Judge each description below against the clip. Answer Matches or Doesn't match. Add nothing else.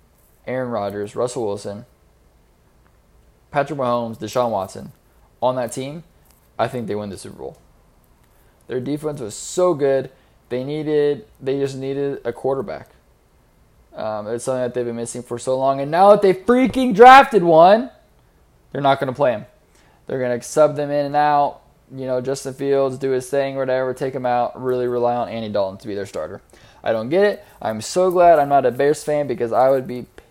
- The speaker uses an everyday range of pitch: Matches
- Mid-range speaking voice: Doesn't match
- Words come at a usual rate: Matches